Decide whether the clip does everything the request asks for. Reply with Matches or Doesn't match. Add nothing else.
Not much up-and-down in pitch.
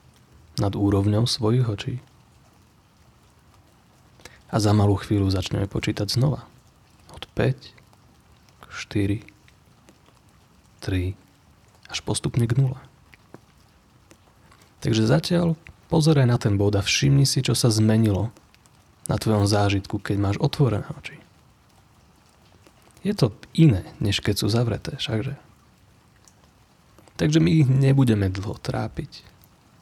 Doesn't match